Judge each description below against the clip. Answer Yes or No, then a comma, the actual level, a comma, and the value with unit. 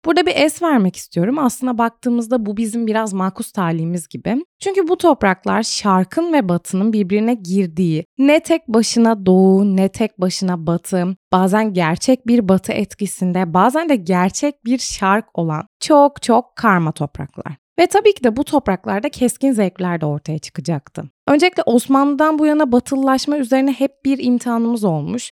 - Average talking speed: No, fast, 155 wpm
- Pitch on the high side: Yes, high, 225 Hz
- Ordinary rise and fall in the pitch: No, wide, 6.6 semitones